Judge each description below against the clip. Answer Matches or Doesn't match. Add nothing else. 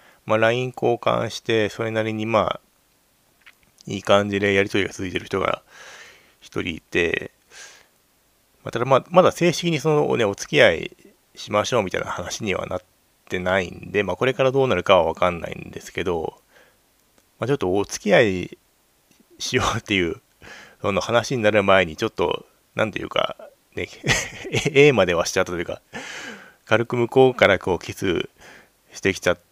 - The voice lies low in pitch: Matches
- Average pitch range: Matches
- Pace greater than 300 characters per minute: Matches